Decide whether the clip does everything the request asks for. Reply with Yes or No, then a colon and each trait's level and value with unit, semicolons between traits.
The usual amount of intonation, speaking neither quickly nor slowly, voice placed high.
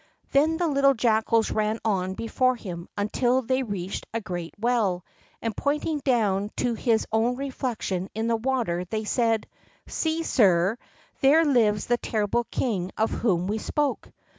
Yes: average, 4.2 semitones; average, 155 wpm; high, 225 Hz